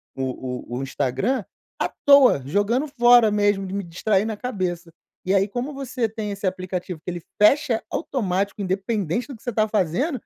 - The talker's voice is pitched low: No, high, 205 Hz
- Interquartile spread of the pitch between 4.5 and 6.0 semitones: Yes, average, 5.0 semitones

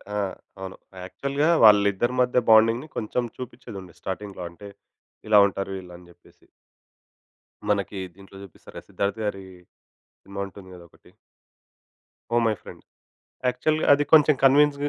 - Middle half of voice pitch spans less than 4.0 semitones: No, average, 4.5 semitones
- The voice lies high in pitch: No, low, 105 Hz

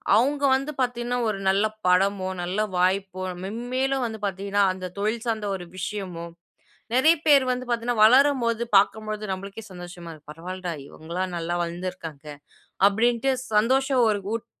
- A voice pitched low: No, high, 205 Hz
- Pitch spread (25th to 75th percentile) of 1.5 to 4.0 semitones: No, average, 4.8 semitones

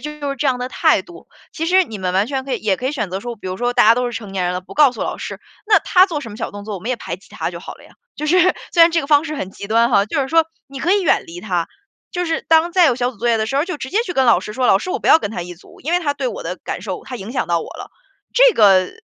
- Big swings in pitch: Yes, wide, 7.6 semitones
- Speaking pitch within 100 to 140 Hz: No, very high, 250 Hz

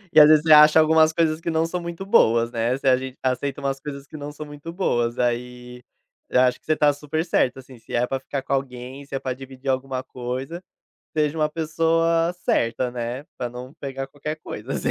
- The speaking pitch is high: No, low, 135 Hz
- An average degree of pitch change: Yes, average, 3.6 semitones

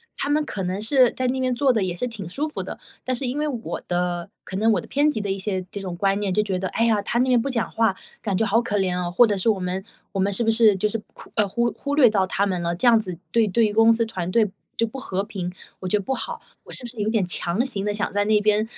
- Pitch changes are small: No, average, 3.7 semitones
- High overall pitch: Yes, high, 210 Hz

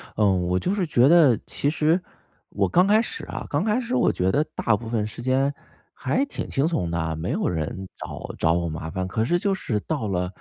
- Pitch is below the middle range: Yes, low, 120 Hz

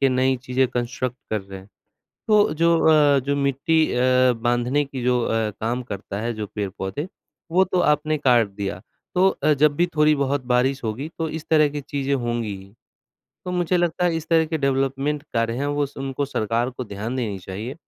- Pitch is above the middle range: No, low, 135 Hz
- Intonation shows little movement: No, average, 4.1 semitones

